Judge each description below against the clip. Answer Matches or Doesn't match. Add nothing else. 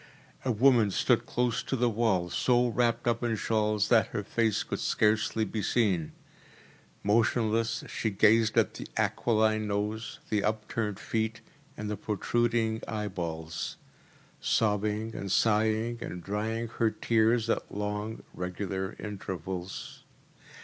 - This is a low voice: Matches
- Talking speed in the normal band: Doesn't match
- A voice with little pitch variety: Matches